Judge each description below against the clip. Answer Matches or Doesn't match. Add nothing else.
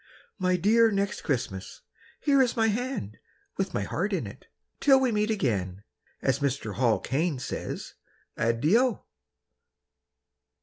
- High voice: Doesn't match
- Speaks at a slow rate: Matches